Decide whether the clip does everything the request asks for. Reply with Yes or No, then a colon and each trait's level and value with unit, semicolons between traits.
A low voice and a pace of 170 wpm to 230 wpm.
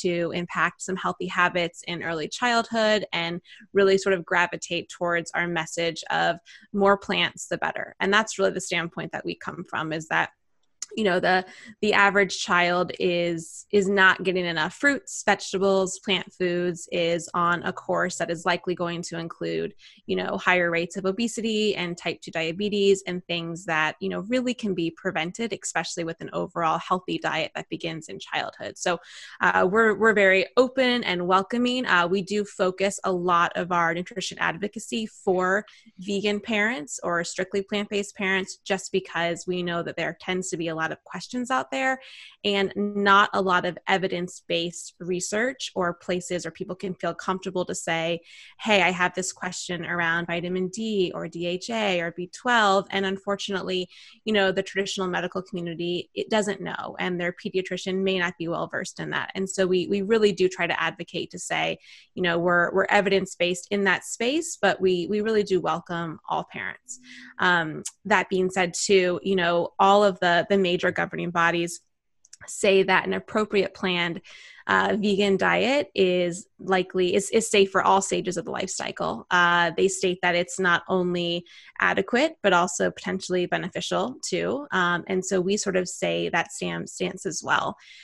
No: medium, 185 Hz; average, 180 wpm